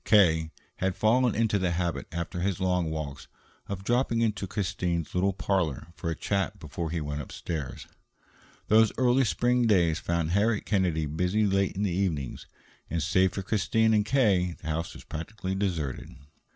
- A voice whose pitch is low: Yes, very low, 95 Hz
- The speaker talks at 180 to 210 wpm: No, average, 165 wpm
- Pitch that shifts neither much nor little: Yes, average, 4.1 semitones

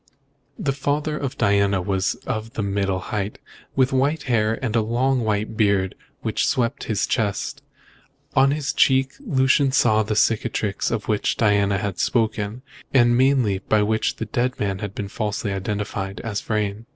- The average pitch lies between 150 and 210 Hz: No, low, 110 Hz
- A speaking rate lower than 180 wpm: Yes, average, 160 wpm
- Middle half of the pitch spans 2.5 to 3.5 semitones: No, average, 4.2 semitones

